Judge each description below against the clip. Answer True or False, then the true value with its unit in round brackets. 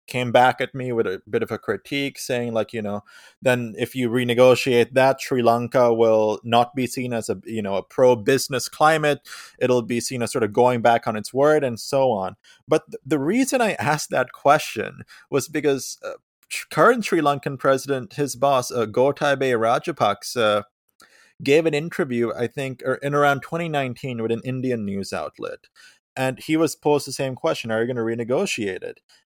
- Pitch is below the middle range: True (130 Hz)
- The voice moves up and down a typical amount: True (3.3 semitones)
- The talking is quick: False (190 wpm)